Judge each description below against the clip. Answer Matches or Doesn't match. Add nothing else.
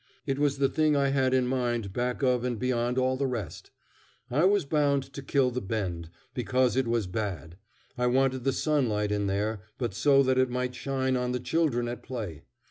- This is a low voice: Matches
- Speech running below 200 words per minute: Doesn't match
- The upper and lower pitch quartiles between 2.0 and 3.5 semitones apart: Matches